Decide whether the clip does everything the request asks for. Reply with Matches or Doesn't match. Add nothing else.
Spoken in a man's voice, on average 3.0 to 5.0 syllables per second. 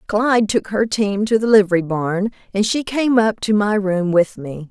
Doesn't match